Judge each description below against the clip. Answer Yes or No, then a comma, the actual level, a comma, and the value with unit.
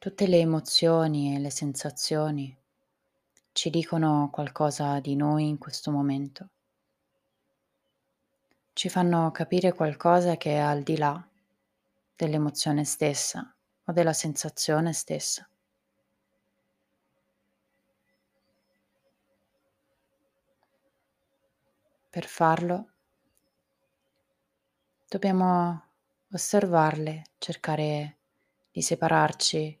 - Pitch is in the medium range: Yes, medium, 155 Hz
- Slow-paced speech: Yes, slow, 70 wpm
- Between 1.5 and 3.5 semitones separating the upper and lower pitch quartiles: Yes, narrow, 2.4 semitones